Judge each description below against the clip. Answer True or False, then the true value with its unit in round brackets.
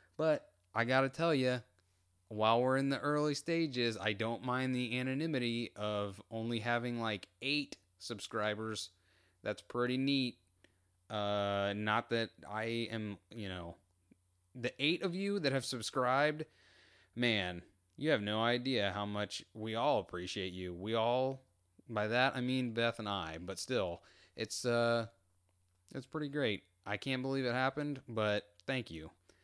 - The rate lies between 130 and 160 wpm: True (150 wpm)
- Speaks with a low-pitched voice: True (110 Hz)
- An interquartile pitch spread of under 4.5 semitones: False (5.4 semitones)